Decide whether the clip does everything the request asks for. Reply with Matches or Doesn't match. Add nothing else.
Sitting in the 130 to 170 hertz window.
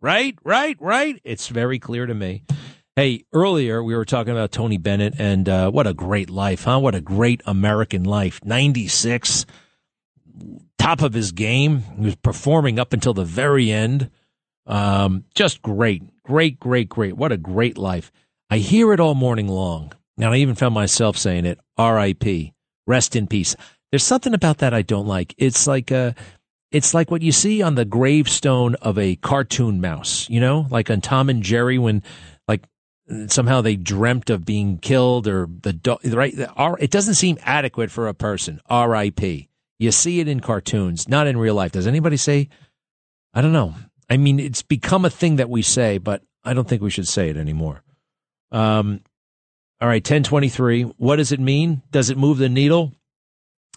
Doesn't match